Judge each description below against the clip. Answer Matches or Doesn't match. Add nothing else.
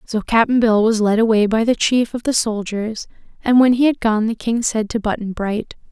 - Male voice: Doesn't match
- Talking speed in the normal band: Doesn't match